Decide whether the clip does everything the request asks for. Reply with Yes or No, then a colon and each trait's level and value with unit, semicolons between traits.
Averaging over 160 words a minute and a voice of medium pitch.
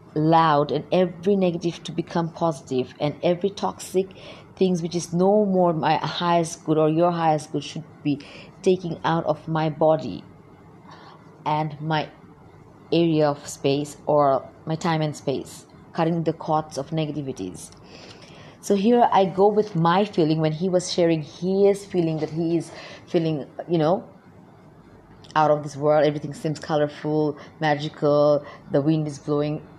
No: average, 150 wpm; medium, 160 Hz